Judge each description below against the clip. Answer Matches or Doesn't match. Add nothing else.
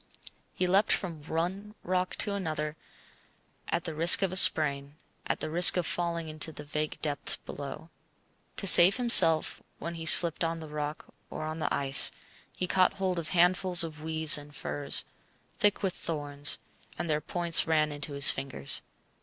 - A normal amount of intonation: Matches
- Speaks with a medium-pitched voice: Matches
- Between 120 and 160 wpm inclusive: Doesn't match